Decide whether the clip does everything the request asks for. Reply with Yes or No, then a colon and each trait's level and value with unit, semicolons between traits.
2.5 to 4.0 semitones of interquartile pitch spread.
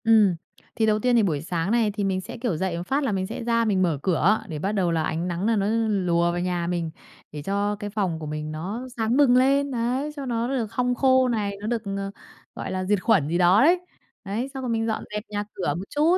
No: average, 4.8 semitones